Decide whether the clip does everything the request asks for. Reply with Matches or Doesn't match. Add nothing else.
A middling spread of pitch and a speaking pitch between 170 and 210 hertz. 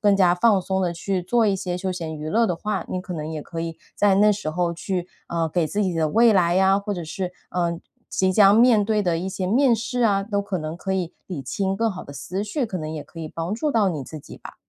Matches